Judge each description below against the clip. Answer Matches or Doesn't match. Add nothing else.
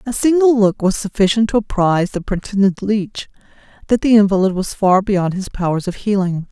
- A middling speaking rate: Matches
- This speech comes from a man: Doesn't match